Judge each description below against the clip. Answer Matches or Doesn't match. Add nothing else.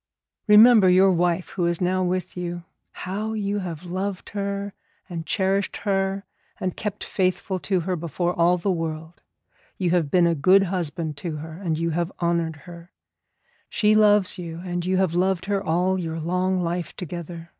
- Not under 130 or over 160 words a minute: Doesn't match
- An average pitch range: Doesn't match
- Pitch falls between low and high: Matches